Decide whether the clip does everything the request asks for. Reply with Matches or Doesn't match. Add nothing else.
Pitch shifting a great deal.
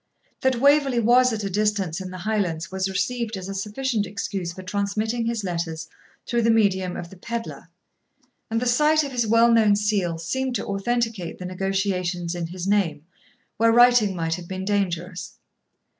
Doesn't match